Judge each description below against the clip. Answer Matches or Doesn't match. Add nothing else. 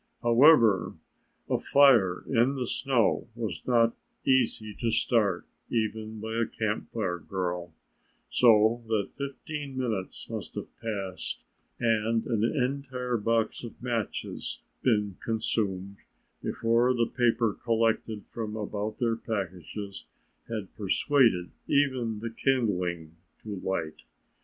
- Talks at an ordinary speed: Doesn't match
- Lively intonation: Doesn't match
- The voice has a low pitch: Matches